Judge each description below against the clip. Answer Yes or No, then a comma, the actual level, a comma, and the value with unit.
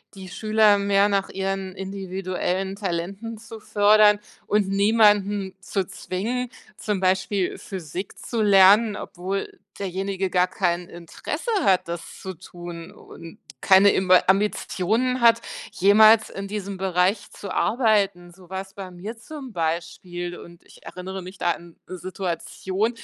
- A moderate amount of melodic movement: No, narrow, 2.3 semitones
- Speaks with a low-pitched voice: No, high, 195 Hz